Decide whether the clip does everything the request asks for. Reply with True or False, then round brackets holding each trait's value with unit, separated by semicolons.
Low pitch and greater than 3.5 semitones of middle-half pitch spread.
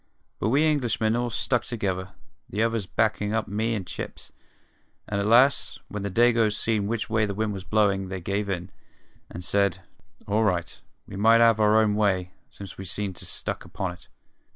False (105 Hz; 2.7 semitones)